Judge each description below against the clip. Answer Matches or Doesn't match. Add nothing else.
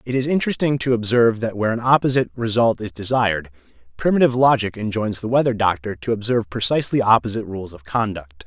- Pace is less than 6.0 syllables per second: Doesn't match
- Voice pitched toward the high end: Doesn't match